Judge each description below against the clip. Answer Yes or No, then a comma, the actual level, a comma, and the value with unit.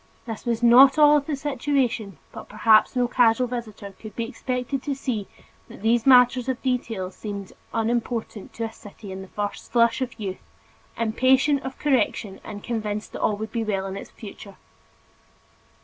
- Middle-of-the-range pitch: No, high, 230 Hz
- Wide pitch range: No, average, 3.4 semitones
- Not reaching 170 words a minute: No, average, 175 wpm